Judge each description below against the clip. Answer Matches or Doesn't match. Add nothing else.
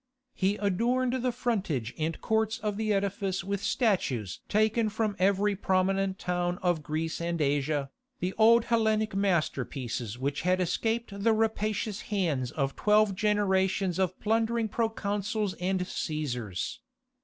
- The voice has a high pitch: Matches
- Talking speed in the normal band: Doesn't match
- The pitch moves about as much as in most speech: Matches